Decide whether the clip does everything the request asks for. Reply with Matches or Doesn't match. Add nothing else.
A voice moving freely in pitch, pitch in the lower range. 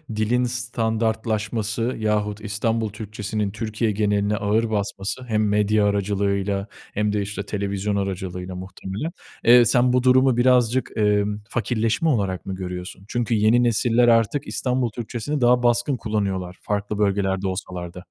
Doesn't match